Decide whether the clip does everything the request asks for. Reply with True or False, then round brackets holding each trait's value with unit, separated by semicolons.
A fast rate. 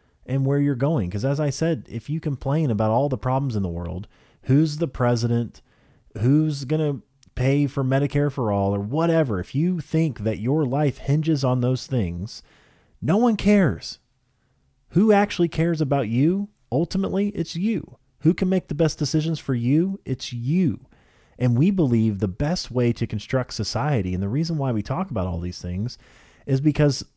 False (185 wpm)